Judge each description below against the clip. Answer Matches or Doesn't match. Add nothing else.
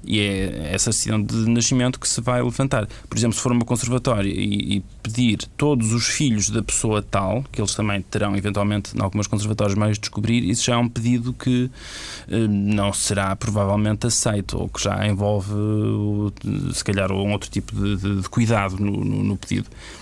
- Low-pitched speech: Matches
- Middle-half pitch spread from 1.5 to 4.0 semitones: Matches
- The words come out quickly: Matches